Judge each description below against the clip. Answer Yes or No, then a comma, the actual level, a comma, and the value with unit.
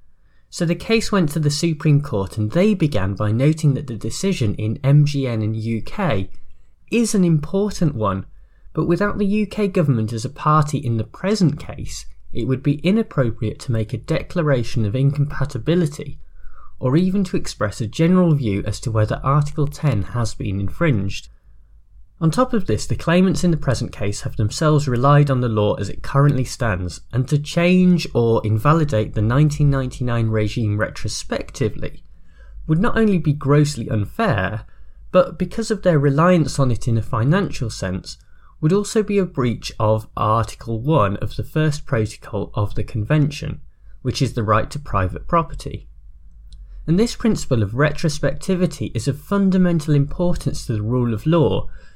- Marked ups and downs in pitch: Yes, wide, 7.1 semitones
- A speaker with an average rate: Yes, average, 165 wpm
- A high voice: No, low, 135 Hz